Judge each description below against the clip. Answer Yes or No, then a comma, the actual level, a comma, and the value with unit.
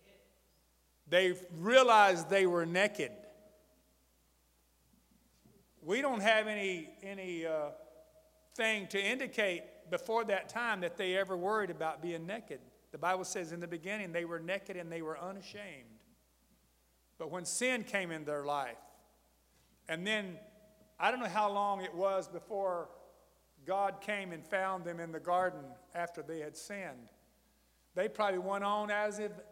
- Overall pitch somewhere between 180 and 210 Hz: Yes, medium, 185 Hz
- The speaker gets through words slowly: No, average, 145 wpm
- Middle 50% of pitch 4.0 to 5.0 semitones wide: Yes, average, 4.5 semitones